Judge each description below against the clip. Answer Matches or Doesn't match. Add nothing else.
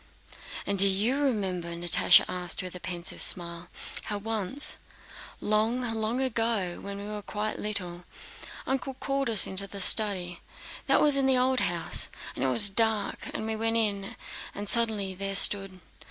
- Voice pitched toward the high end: Matches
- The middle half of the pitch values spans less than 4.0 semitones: Matches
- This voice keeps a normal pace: Matches